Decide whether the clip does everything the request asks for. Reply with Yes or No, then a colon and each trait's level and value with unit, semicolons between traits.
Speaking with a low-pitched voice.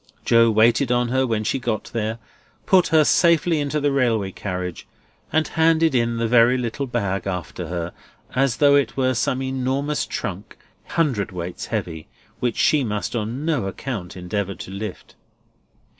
Yes: low, 120 Hz